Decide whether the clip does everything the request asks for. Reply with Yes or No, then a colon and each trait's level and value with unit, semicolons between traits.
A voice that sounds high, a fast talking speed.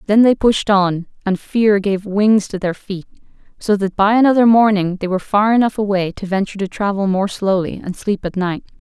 Yes: high, 200 Hz; fast, 210 wpm